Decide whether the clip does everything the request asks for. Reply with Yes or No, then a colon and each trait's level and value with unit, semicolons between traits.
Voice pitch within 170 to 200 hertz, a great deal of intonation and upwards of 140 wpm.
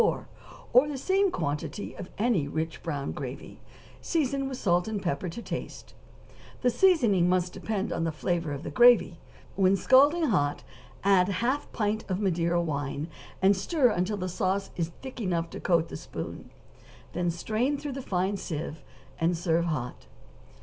Yes: medium, 185 Hz; wide, 6.2 semitones; average, 170 wpm